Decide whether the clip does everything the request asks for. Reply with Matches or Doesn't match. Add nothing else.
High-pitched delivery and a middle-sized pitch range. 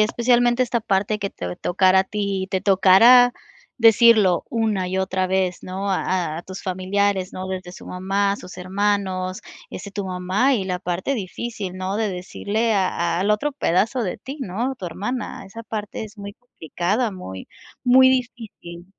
Matches